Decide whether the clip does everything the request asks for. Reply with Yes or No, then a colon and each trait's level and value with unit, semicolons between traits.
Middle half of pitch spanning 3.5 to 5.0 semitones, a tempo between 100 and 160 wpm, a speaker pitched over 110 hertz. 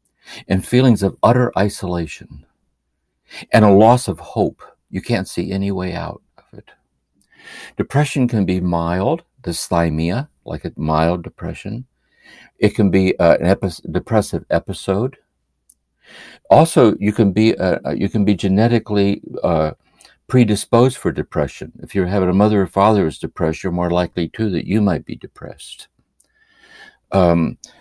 No: average, 4.5 semitones; average, 140 wpm; very low, 95 Hz